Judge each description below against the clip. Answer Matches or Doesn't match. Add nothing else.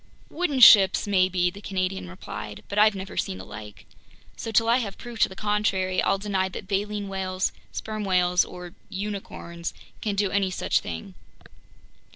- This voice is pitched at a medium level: Doesn't match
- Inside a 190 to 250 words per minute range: Doesn't match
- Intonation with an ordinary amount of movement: Doesn't match